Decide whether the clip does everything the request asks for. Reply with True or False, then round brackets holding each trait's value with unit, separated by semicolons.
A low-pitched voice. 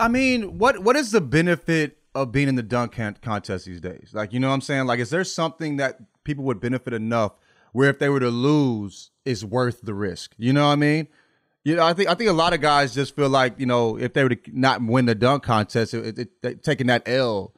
True (130 Hz)